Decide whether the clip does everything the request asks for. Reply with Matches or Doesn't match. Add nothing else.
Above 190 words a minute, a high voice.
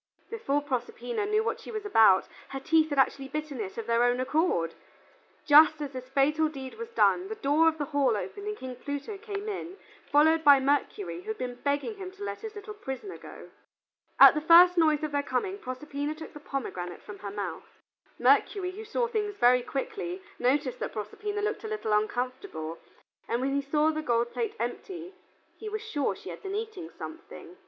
Matches